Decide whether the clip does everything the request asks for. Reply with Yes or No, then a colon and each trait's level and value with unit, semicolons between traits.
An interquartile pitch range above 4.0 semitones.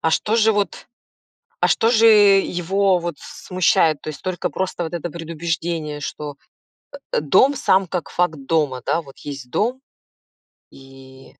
Yes: average, 4.5 semitones